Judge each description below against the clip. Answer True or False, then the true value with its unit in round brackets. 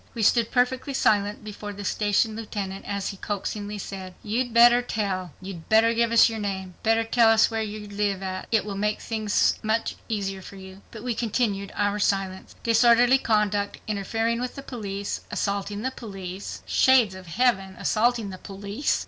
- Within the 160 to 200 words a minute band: True (165 wpm)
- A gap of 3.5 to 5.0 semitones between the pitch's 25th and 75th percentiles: False (2.7 semitones)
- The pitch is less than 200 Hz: False (210 Hz)